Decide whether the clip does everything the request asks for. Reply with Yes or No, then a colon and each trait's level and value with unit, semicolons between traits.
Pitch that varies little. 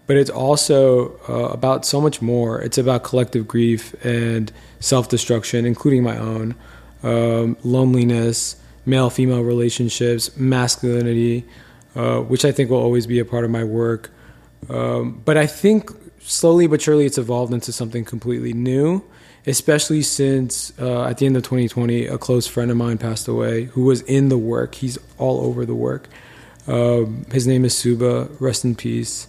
Yes: narrow, 2.1 semitones